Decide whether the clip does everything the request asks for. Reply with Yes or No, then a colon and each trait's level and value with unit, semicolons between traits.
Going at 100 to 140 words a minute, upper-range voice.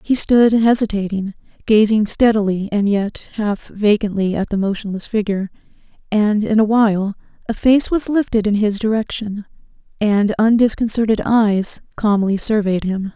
Yes: slow, 135 wpm; high, 210 Hz